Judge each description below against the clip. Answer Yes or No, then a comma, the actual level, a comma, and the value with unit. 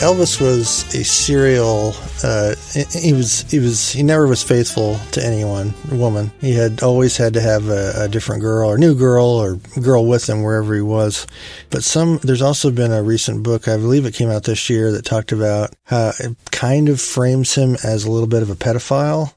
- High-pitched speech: No, low, 120 Hz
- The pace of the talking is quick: Yes, fast, 210 wpm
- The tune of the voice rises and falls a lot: No, average, 3.3 semitones